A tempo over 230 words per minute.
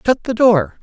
No: fast, 215 wpm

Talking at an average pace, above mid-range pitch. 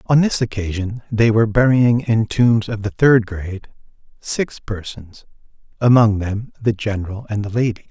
No: average, 160 wpm; low, 110 Hz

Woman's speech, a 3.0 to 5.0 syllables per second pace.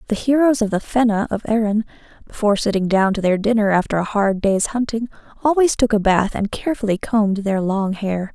No: female; 5.7 syllables/s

